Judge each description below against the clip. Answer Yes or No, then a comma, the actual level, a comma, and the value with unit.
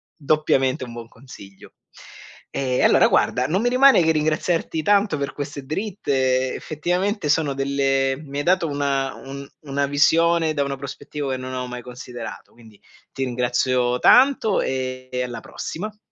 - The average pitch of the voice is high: No, medium, 140 Hz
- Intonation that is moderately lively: Yes, average, 3.7 semitones